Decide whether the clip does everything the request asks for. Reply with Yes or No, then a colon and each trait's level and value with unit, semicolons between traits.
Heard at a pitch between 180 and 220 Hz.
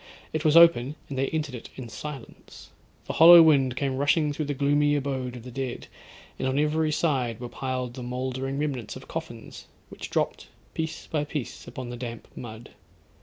No: low, 135 Hz